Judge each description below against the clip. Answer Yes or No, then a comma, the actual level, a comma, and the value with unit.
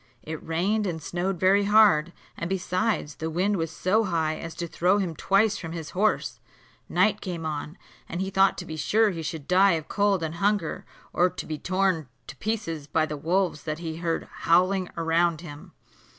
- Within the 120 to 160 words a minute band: No, average, 190 wpm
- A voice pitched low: No, medium, 175 Hz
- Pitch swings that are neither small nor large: Yes, average, 3.3 semitones